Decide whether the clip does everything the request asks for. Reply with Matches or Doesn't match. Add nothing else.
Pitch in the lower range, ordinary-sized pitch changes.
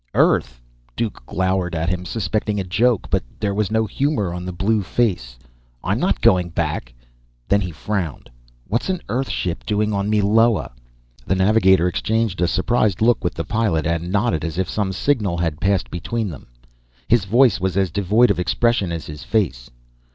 Matches